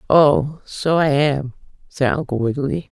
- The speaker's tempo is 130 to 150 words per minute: Yes, average, 140 wpm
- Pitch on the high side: No, medium, 145 Hz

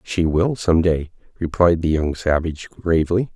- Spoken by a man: Yes, male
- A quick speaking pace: No, average, 160 wpm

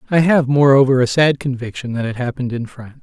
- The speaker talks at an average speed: No, fast, 220 wpm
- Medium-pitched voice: No, low, 130 Hz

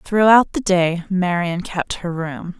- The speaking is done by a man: No, female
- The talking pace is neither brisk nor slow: Yes, average, 160 wpm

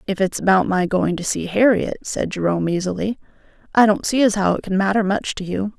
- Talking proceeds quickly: Yes, fast, 230 wpm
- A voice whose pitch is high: Yes, high, 195 Hz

